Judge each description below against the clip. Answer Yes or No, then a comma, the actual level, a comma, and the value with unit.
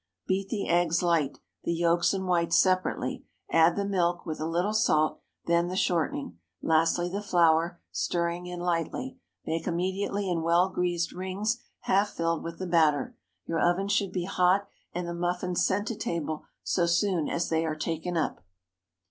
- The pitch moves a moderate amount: No, narrow, 2.0 semitones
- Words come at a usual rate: Yes, average, 165 wpm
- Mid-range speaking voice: Yes, medium, 175 Hz